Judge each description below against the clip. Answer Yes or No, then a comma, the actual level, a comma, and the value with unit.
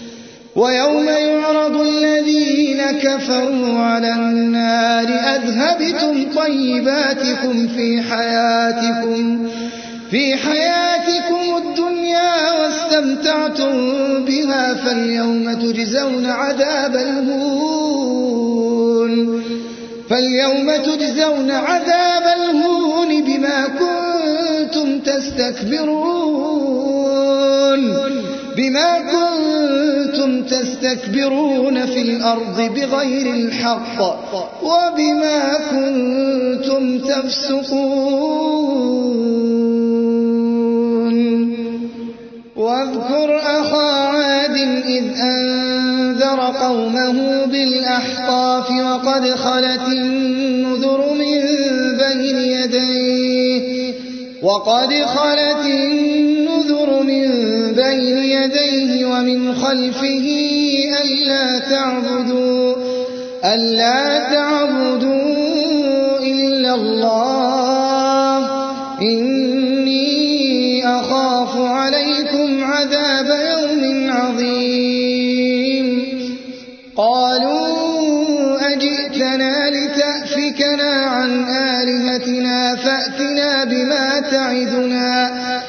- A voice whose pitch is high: Yes, very high, 265 Hz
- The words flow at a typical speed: No, slow, 55 wpm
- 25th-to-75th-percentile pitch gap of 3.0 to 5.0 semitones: No, narrow, 2.4 semitones